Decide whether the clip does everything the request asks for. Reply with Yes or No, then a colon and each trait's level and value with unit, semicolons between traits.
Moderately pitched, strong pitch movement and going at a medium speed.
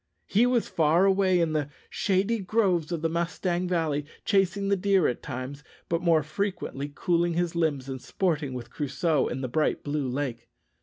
No: medium, 165 Hz; average, 4.4 semitones; average, 175 wpm